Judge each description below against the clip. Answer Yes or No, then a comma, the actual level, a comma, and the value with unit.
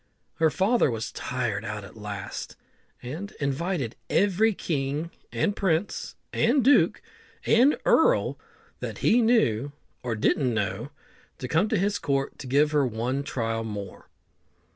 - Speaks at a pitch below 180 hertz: Yes, medium, 140 Hz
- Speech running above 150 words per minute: No, average, 140 wpm